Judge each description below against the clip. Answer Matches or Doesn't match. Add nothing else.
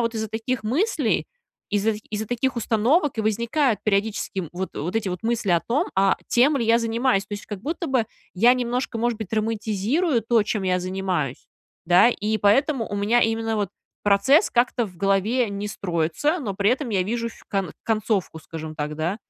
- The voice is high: Matches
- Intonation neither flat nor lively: Matches